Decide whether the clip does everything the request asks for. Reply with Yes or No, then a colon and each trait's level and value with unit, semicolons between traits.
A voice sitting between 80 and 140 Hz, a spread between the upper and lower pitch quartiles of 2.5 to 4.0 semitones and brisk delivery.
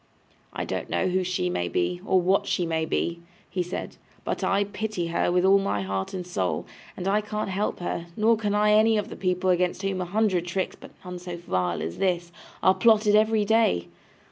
No: medium, 185 Hz; average, 3.3 semitones; fast, 215 wpm